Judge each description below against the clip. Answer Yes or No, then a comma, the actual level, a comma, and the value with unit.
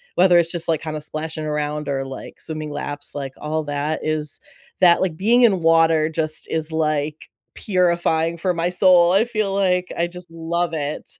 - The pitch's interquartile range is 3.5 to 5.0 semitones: No, narrow, 2.6 semitones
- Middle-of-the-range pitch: Yes, medium, 160 Hz